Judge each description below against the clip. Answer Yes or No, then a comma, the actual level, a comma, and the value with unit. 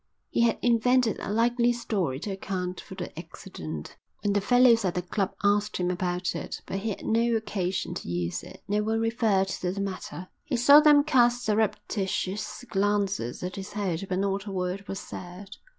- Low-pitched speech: No, high, 200 Hz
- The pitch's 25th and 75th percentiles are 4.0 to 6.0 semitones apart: No, average, 3.6 semitones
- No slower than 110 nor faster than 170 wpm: No, average, 190 wpm